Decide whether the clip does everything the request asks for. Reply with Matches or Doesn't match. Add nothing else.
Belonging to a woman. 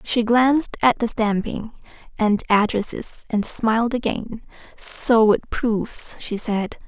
Matches